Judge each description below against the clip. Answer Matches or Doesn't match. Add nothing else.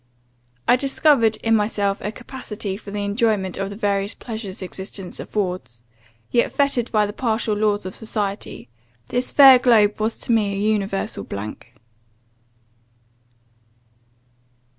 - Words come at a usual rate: Doesn't match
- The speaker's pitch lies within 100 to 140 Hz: Doesn't match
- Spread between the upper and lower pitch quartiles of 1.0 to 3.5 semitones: Matches